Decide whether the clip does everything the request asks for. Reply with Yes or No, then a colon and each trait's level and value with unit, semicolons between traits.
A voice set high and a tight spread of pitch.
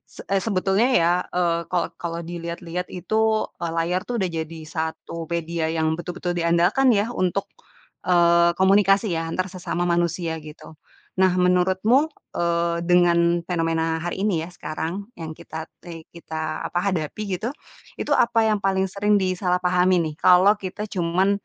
No: medium, 175 Hz; narrow, 1.9 semitones